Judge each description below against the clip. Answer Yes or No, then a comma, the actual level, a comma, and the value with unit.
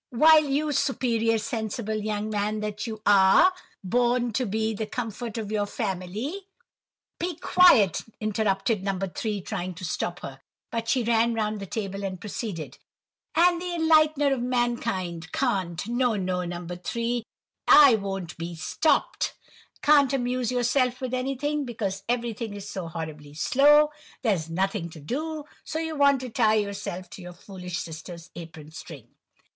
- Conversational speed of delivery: Yes, average, 150 wpm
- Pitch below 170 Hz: No, high, 220 Hz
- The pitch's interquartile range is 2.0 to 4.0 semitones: No, average, 5.2 semitones